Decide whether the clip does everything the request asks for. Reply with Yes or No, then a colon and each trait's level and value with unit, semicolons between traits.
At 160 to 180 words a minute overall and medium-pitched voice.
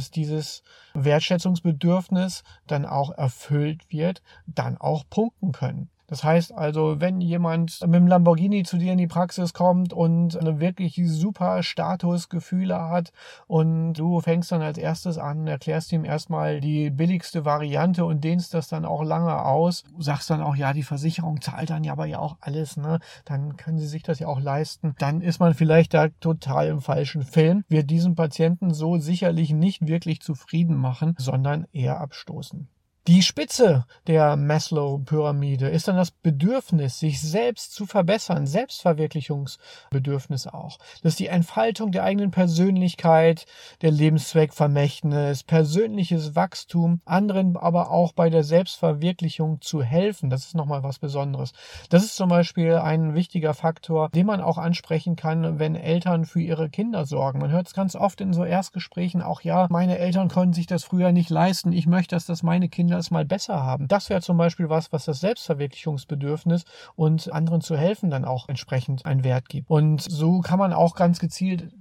Yes: average, 170 wpm; medium, 165 Hz